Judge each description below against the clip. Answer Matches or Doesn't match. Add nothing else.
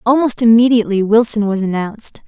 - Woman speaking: Matches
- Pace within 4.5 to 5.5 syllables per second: Doesn't match